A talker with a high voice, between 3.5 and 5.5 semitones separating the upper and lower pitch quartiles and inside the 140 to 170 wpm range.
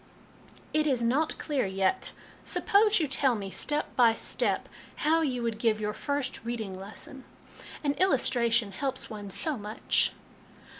Yes: high, 240 Hz; average, 5.2 semitones; average, 150 wpm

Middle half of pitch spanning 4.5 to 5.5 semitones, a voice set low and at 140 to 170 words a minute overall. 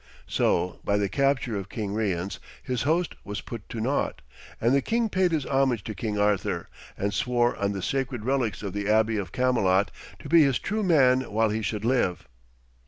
No: average, 4.8 semitones; low, 115 Hz; average, 195 wpm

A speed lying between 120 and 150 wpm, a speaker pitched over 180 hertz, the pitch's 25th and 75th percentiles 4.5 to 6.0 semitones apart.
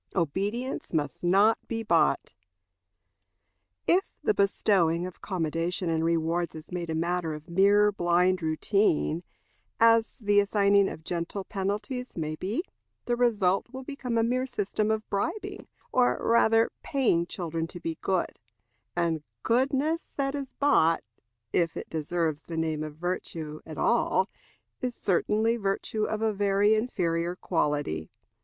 Yes: average, 140 wpm; high, 190 Hz; average, 5.1 semitones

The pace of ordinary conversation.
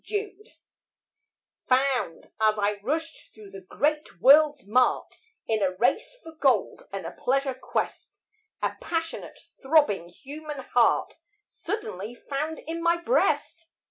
No: slow, 125 wpm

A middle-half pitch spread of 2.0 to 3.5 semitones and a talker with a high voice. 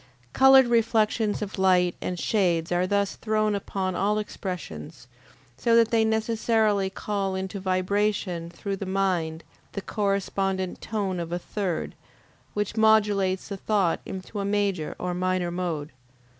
Yes: narrow, 2.6 semitones; high, 195 Hz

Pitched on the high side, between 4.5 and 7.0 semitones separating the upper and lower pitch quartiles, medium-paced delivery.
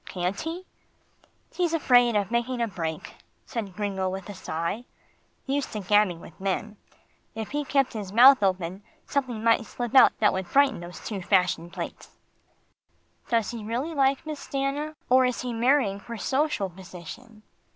Yes: high, 225 Hz; wide, 5.6 semitones; average, 160 wpm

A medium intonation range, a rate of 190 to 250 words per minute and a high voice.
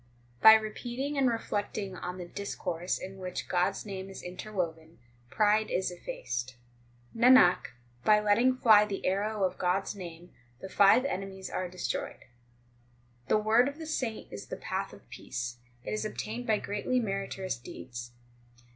No: average, 3.3 semitones; average, 160 wpm; high, 195 Hz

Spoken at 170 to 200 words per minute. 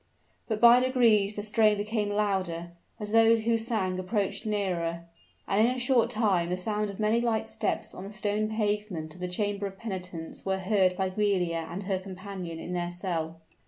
Yes: average, 190 wpm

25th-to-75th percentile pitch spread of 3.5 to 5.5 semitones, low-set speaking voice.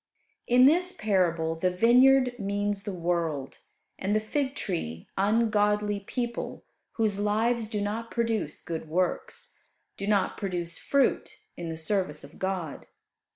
No: average, 4.5 semitones; high, 205 Hz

